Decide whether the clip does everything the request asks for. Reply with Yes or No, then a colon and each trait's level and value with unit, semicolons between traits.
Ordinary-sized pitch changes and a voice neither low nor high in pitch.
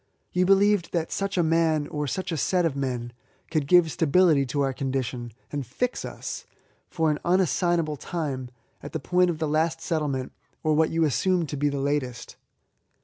Yes: average, 3.9 semitones; medium, 155 Hz